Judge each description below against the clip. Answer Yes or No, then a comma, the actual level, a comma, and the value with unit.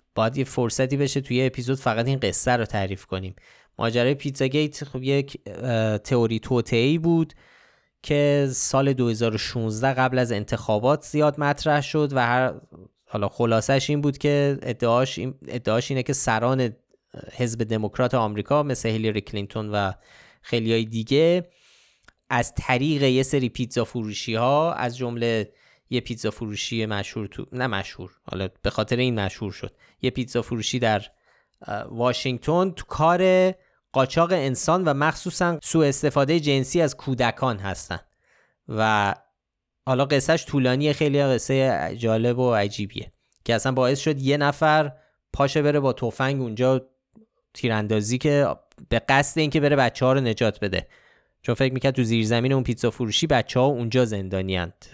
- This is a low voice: Yes, low, 125 Hz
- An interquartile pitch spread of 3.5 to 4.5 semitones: Yes, average, 3.8 semitones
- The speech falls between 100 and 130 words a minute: No, average, 145 wpm